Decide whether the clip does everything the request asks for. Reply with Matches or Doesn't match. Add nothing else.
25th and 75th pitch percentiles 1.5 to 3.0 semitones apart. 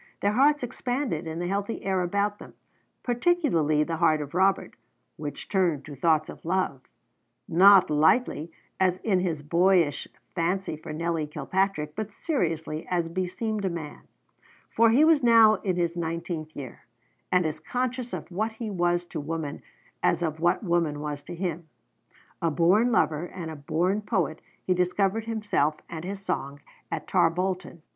Doesn't match